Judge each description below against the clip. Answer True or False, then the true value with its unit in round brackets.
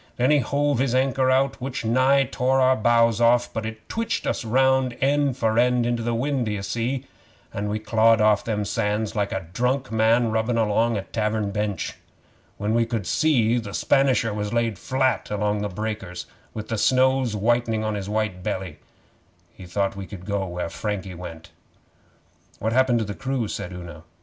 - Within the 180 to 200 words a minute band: True (190 wpm)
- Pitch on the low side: True (115 Hz)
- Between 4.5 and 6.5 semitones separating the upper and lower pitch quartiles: False (3.5 semitones)